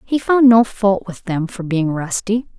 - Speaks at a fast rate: Yes, fast, 210 wpm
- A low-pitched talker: No, high, 200 Hz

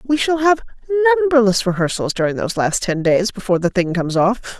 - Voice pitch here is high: Yes, high, 225 Hz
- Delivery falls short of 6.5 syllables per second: No, 6.6 syllables/s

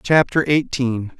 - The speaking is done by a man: Yes, male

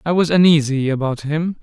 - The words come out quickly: No, average, 185 wpm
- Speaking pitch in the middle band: Yes, medium, 150 Hz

